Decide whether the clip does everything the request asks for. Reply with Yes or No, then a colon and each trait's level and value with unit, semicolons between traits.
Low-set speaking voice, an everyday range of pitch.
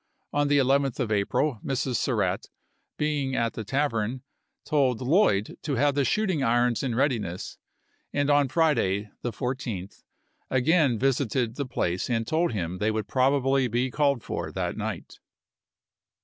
Yes: low, 130 Hz; average, 4.0 semitones